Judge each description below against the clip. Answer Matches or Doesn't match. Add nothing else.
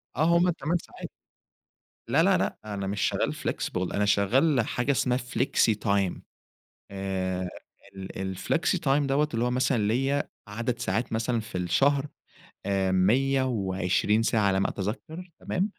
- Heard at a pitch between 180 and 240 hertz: Doesn't match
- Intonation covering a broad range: Matches